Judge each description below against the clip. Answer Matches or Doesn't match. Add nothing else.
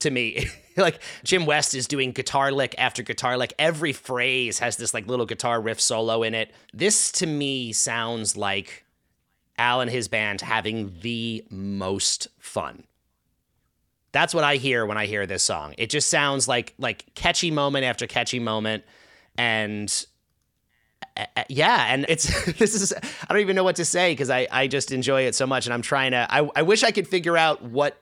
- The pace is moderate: Matches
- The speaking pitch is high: Doesn't match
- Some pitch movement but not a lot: Matches